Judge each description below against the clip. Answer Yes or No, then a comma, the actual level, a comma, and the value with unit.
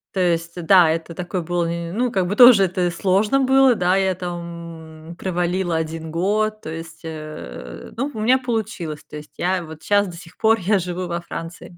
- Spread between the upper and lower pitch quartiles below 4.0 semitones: Yes, average, 3.3 semitones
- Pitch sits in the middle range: Yes, medium, 175 Hz